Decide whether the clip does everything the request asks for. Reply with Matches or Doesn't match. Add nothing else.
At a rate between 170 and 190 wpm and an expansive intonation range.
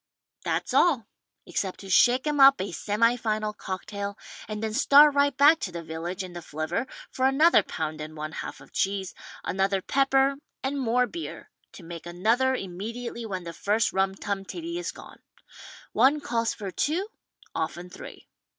Matches